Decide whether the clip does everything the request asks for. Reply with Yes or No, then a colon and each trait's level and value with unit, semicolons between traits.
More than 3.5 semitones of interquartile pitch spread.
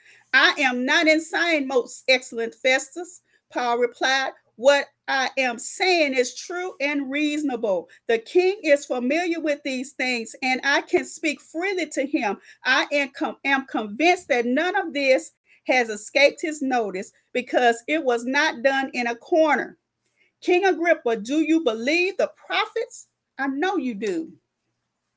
Yes: average, 4.3 semitones